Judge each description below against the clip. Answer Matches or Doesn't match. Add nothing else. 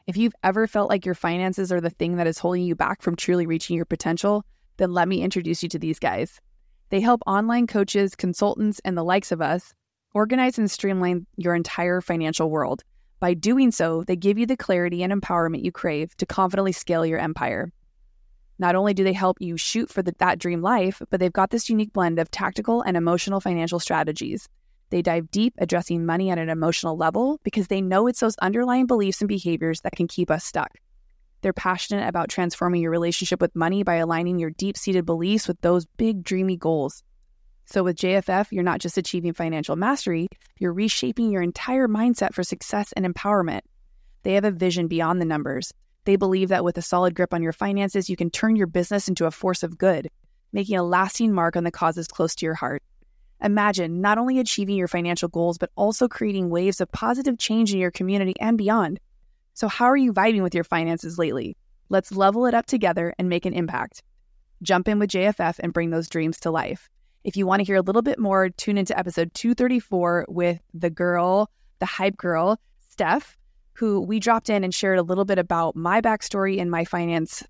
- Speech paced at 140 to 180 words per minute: Doesn't match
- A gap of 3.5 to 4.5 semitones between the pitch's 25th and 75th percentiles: Doesn't match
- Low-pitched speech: Doesn't match